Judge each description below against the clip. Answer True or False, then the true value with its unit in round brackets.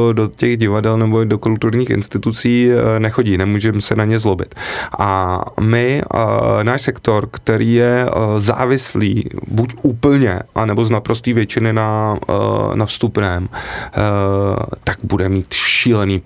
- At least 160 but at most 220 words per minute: False (120 wpm)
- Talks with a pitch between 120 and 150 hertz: False (110 Hz)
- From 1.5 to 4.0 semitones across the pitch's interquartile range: True (2.6 semitones)